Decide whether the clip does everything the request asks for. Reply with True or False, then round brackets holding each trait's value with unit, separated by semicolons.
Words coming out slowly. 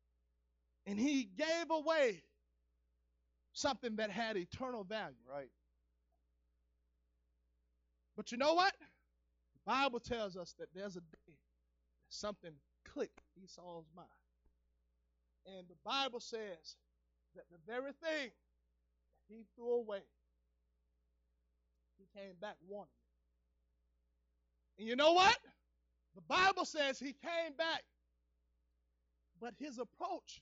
True (115 wpm)